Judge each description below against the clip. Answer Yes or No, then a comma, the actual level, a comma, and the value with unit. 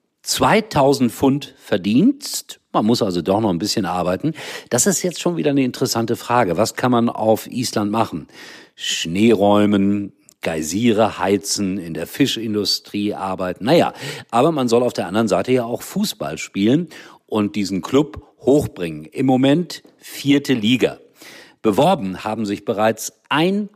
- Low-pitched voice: Yes, low, 115 Hz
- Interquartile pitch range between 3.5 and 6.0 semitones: Yes, average, 5.2 semitones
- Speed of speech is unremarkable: Yes, average, 145 wpm